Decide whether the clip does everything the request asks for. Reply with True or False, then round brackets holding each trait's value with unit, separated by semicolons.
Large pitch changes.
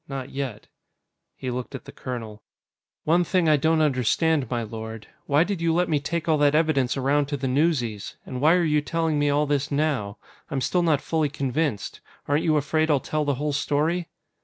False (3.3 semitones)